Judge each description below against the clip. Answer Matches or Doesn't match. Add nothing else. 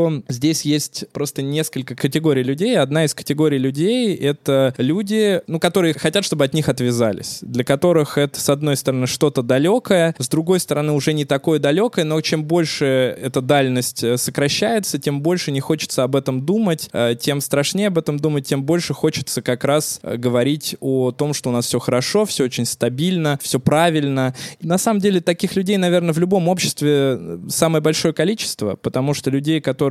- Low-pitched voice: Doesn't match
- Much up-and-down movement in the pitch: Doesn't match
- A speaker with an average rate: Doesn't match